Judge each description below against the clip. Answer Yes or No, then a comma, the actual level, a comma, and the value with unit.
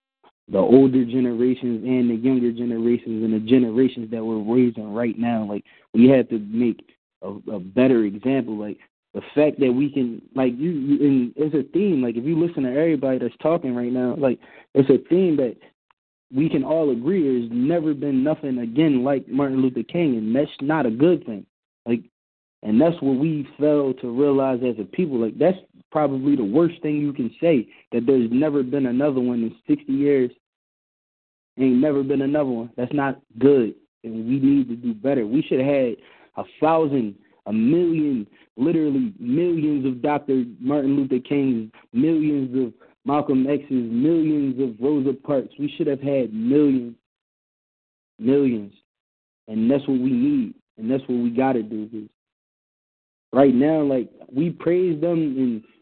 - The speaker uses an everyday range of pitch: Yes, average, 3.6 semitones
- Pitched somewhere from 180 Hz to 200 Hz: No, low, 135 Hz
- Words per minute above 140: Yes, average, 175 wpm